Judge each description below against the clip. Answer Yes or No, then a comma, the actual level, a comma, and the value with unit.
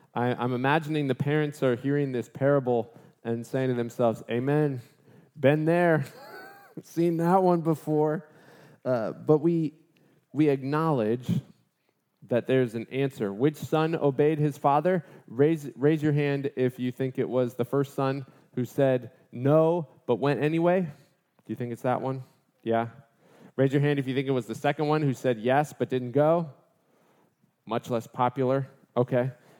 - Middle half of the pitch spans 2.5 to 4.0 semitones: Yes, average, 3.7 semitones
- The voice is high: No, medium, 140 Hz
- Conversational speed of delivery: Yes, average, 160 wpm